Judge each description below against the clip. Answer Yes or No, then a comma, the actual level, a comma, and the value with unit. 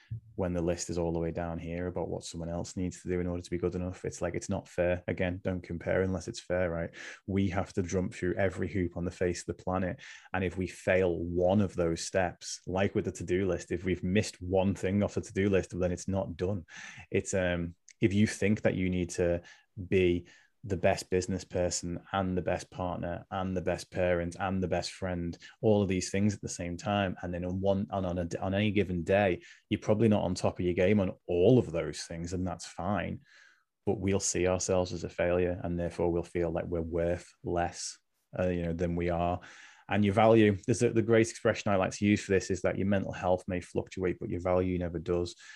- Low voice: Yes, very low, 90 Hz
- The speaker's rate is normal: No, fast, 240 wpm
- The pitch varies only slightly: Yes, narrow, 1.9 semitones